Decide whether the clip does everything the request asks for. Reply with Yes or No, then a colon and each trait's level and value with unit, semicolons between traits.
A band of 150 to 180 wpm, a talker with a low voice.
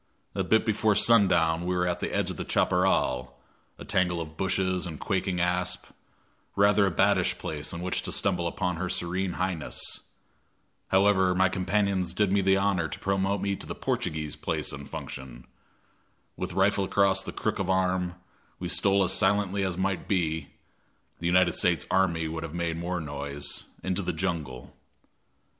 Yes: average, 170 wpm; very low, 90 Hz